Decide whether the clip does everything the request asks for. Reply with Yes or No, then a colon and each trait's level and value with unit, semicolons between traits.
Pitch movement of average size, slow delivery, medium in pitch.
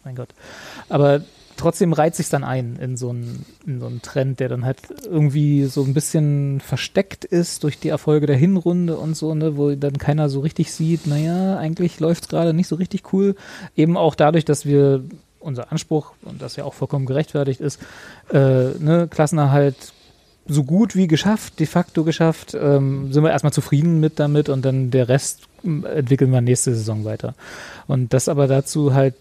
No: average, 3.0 semitones; fast, 190 wpm; medium, 150 Hz